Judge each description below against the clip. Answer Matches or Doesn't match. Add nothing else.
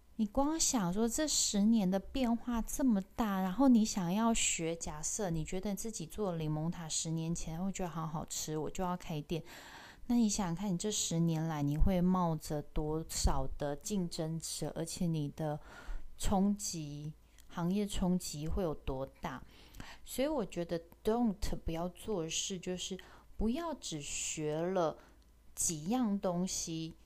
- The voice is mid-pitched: Matches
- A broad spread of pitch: Doesn't match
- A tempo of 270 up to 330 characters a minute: Doesn't match